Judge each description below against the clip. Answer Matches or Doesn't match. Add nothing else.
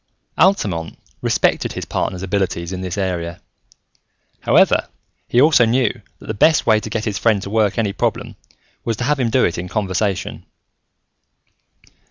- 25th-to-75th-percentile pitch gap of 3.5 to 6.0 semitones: Matches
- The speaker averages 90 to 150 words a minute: Doesn't match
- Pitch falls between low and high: Doesn't match